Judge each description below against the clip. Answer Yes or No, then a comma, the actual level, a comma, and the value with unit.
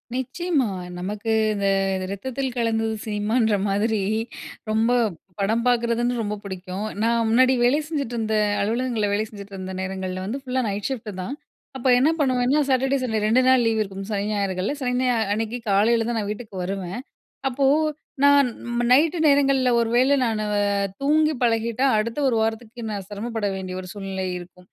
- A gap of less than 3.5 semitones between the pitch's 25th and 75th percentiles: No, average, 3.9 semitones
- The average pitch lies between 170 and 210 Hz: No, high, 225 Hz